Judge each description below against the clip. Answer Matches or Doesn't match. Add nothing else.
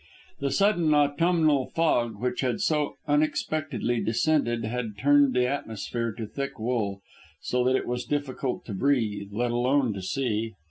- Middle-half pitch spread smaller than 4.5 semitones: Matches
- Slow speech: Doesn't match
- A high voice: Doesn't match